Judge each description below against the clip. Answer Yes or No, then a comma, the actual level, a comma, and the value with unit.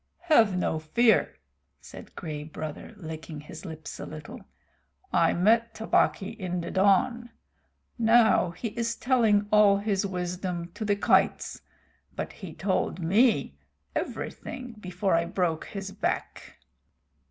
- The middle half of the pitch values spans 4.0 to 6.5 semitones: Yes, average, 4.7 semitones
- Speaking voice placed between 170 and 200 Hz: Yes, high, 190 Hz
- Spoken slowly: Yes, slow, 130 wpm